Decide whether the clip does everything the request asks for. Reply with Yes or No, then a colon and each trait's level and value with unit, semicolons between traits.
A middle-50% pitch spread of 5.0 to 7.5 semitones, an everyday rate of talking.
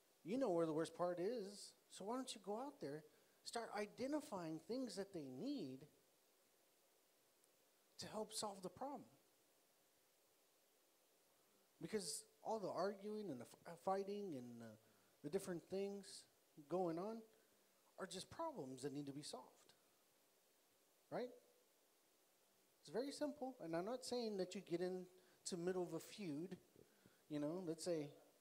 Yes: average, 5.3 semitones; average, 145 wpm